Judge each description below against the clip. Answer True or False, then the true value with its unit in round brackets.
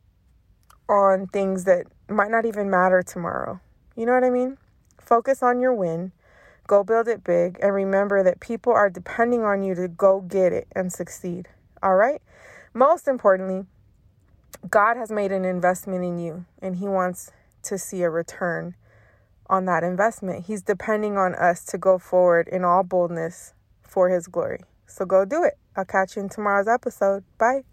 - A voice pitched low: False (190 Hz)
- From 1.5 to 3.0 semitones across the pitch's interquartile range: True (2.7 semitones)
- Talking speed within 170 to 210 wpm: True (175 wpm)